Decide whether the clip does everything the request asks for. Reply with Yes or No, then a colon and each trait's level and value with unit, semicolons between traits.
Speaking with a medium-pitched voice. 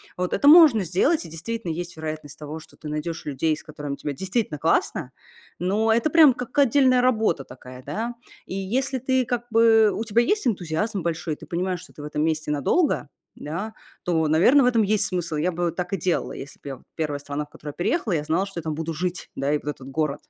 Yes: medium, 175 Hz